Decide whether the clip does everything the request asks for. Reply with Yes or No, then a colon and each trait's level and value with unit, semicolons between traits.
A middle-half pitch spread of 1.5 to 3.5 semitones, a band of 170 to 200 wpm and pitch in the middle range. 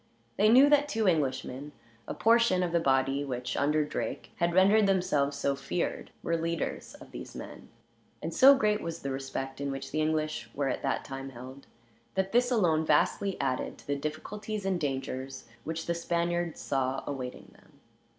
No: wide, 5.6 semitones; average, 180 wpm; medium, 155 Hz